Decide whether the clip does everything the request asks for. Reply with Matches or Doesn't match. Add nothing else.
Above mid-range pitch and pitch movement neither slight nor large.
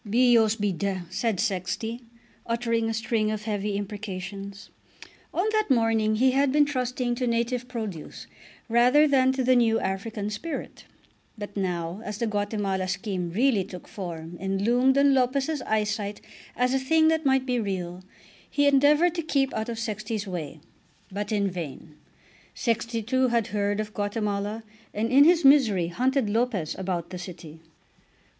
Matches